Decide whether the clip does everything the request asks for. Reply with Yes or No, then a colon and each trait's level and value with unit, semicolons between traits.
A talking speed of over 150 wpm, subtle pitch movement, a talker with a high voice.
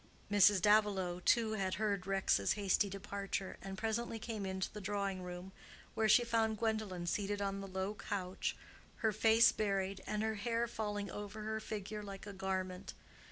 Yes: average, 165 wpm; narrow, 2.1 semitones; high, 205 Hz